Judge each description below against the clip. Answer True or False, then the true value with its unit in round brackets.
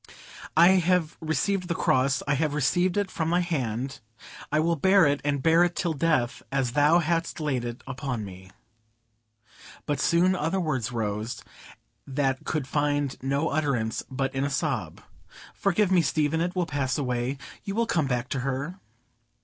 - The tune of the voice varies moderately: True (4.2 semitones)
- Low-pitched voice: False (145 Hz)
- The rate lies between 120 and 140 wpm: False (165 wpm)